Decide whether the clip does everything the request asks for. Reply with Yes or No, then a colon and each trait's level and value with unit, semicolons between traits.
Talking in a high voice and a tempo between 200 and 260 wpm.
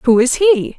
Yes: very high, 285 Hz; fast, 230 wpm